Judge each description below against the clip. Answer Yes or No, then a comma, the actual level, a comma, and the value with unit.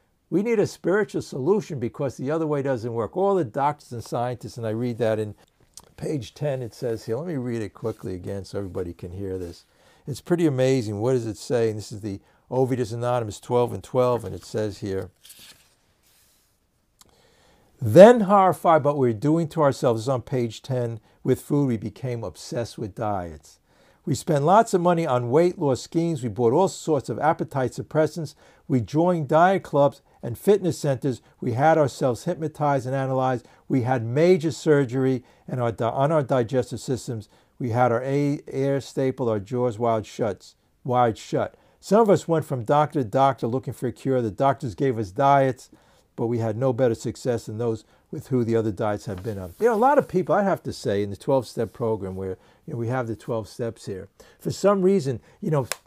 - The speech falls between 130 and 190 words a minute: No, average, 200 wpm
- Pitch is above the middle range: No, low, 125 Hz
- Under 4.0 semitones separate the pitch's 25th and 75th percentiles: No, average, 4.4 semitones